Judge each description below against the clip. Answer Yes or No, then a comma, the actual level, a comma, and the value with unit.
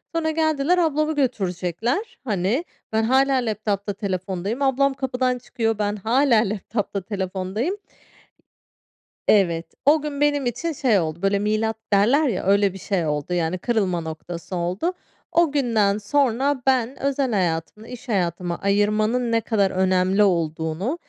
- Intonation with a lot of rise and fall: Yes, wide, 6.1 semitones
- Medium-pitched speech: No, high, 215 Hz